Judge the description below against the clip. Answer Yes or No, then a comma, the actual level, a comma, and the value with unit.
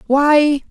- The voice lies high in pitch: Yes, very high, 285 Hz